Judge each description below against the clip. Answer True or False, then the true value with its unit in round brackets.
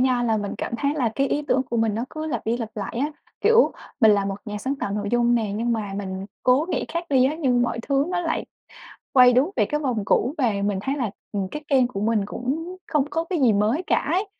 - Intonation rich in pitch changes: False (5.0 semitones)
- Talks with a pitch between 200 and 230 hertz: False (245 Hz)